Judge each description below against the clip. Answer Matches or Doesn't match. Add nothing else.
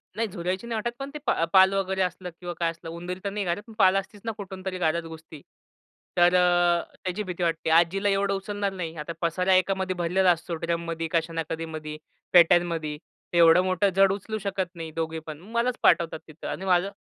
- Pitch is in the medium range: Matches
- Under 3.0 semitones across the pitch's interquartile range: Matches